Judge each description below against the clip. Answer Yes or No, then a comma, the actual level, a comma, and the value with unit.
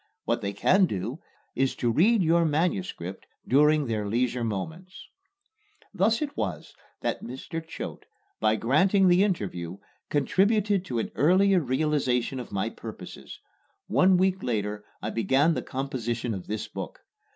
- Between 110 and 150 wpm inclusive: Yes, average, 140 wpm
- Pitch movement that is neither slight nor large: No, wide, 8.4 semitones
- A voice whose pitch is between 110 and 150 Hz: Yes, low, 135 Hz